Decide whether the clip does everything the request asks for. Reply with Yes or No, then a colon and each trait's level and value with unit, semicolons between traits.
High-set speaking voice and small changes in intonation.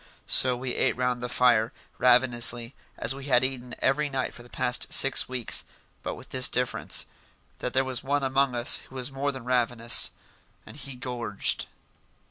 No: low, 125 Hz; narrow, 1.6 semitones